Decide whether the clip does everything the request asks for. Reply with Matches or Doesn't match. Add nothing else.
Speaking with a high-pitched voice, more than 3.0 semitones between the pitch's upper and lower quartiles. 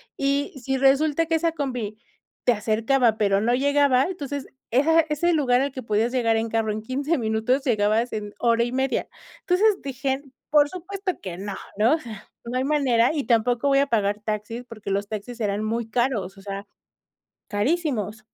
Matches